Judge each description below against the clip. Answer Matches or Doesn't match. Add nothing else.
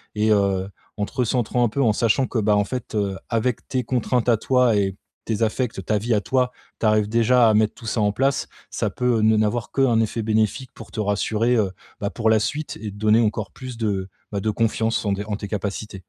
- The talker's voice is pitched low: Matches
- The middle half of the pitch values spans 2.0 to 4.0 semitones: Matches